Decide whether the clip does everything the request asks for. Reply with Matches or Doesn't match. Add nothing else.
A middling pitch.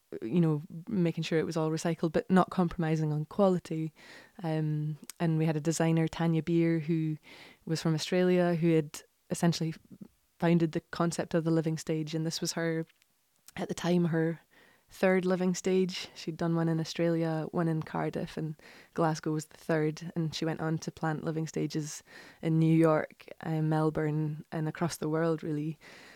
Matches